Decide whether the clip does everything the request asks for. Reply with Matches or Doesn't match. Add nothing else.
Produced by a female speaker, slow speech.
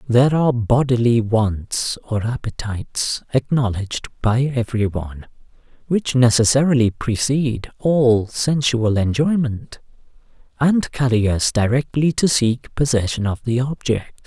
Doesn't match